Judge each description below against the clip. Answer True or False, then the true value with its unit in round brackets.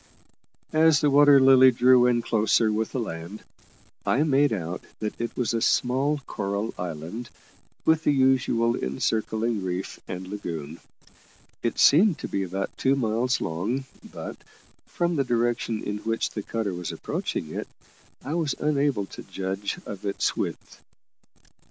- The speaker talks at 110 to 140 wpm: False (150 wpm)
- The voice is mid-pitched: False (115 Hz)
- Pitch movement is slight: False (5.2 semitones)